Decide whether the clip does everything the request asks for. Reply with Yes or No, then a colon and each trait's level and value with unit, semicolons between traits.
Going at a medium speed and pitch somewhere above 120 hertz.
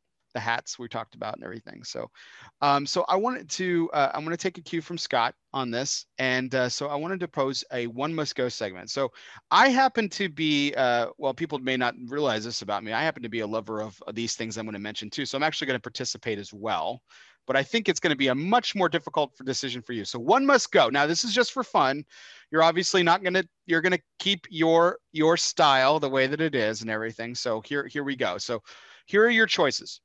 No: fast, 250 wpm; medium, 140 Hz